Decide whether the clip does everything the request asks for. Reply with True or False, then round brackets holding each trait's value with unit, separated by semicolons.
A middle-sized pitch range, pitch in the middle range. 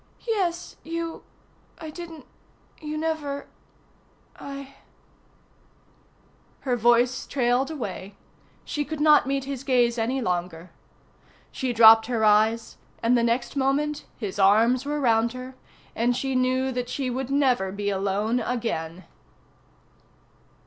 False (3.8 semitones; 250 Hz)